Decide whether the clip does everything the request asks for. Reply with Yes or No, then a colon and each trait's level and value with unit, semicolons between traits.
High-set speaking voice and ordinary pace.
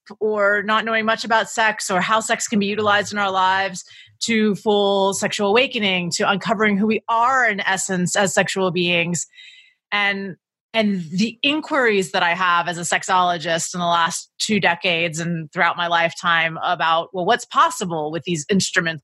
Yes: high, 195 Hz; average, 175 wpm